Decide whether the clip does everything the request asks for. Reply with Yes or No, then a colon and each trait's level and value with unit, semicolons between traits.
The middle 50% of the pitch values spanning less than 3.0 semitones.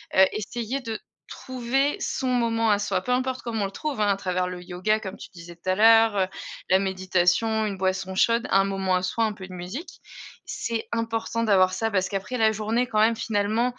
No: average, 3.5 semitones